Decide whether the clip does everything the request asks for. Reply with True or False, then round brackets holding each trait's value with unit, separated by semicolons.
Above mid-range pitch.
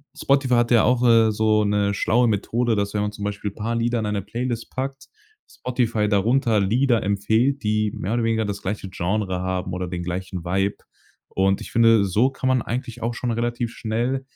False (110 Hz)